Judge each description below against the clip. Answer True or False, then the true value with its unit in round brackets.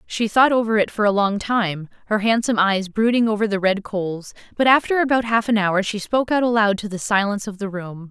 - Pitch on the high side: True (210 Hz)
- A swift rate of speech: True (235 wpm)